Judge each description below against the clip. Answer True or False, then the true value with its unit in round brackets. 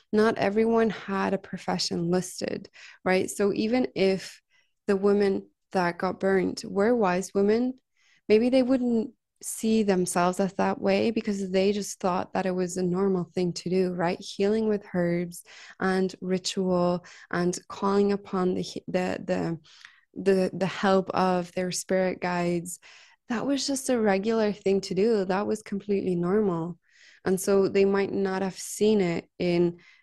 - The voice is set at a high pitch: True (195 Hz)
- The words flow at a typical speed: True (155 wpm)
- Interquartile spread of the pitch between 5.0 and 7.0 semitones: False (2.4 semitones)